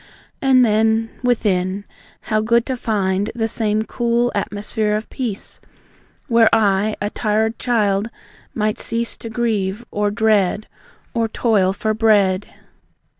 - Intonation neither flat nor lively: No, narrow, 2.0 semitones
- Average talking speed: No, slow, 125 wpm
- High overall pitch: Yes, high, 215 Hz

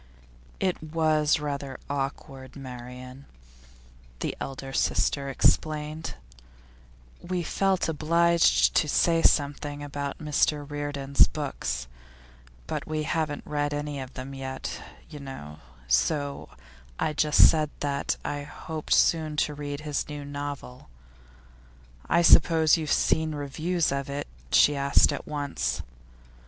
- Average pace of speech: No, slow, 120 wpm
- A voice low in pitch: No, medium, 145 Hz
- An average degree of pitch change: No, narrow, 1.9 semitones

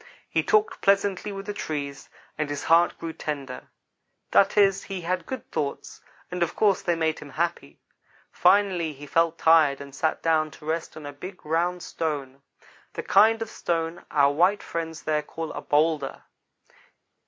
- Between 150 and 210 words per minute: Yes, average, 170 wpm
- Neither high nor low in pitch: Yes, medium, 165 Hz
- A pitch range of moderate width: Yes, average, 3.5 semitones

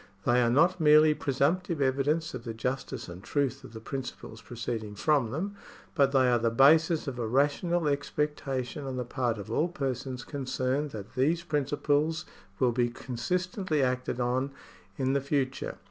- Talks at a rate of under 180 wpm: Yes, average, 165 wpm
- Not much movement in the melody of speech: No, average, 3.5 semitones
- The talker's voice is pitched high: No, low, 135 Hz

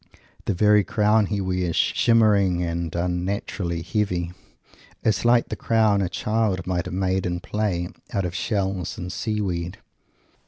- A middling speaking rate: Yes, average, 150 wpm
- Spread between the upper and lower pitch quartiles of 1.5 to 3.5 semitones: Yes, average, 3.1 semitones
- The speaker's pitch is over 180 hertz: No, very low, 95 Hz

